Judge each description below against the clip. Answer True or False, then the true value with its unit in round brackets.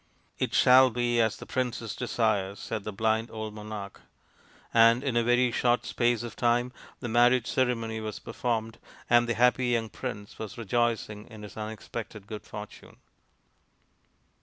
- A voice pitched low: True (115 Hz)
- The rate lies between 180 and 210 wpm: False (160 wpm)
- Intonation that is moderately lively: False (1.9 semitones)